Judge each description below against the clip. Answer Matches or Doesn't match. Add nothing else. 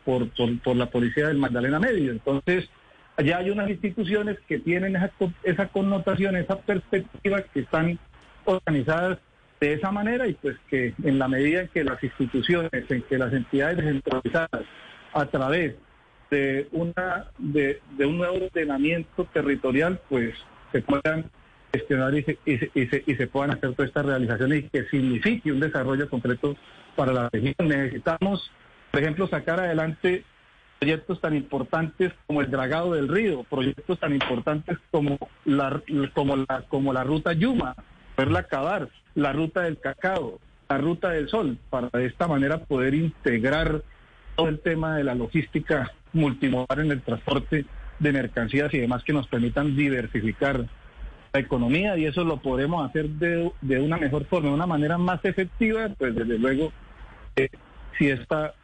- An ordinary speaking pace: Matches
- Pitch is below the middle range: Doesn't match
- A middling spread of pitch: Matches